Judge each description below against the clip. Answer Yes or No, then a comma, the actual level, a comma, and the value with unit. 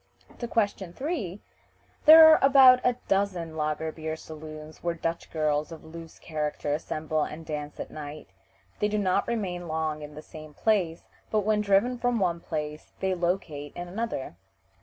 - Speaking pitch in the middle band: Yes, medium, 170 Hz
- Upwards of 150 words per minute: Yes, average, 165 wpm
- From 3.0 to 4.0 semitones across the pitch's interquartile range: No, average, 5.1 semitones